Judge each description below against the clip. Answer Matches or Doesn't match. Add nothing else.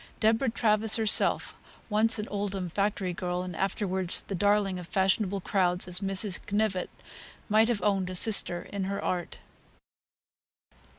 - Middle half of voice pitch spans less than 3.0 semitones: Matches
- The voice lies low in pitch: Doesn't match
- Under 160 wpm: Matches